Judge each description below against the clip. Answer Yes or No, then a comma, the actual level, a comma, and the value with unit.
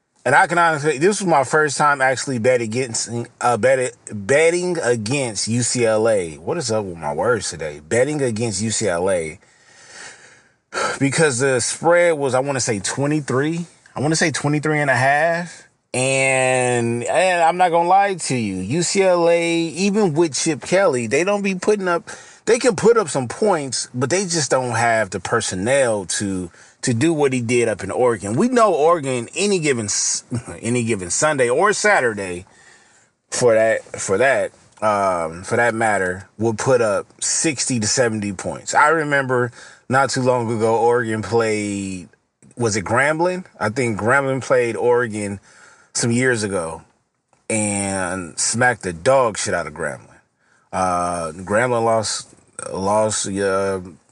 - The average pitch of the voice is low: Yes, low, 125 Hz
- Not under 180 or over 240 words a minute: No, average, 155 wpm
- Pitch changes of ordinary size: No, wide, 6.2 semitones